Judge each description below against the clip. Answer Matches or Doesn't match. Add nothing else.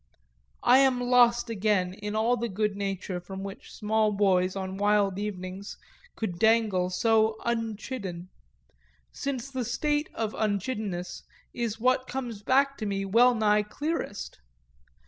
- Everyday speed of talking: Doesn't match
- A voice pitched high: Matches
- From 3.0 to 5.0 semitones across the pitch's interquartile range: Matches